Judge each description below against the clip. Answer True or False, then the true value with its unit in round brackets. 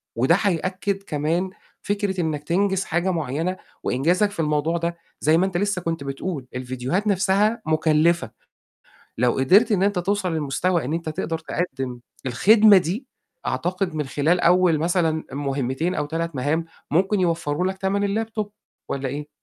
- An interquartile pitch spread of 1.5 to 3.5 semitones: False (4.3 semitones)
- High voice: False (170 Hz)